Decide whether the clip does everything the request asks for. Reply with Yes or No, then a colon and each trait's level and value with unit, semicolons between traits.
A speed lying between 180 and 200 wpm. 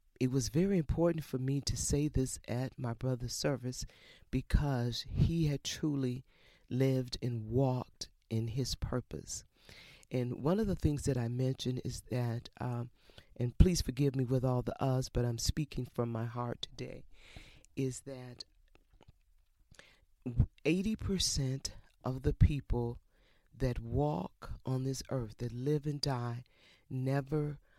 No: average, 140 wpm